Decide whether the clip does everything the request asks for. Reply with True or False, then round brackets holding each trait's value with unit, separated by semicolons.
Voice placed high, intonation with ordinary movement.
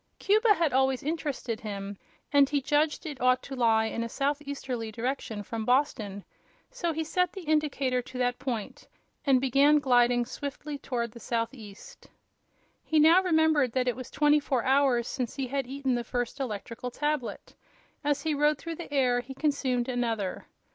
True (265 Hz; 3.5 semitones)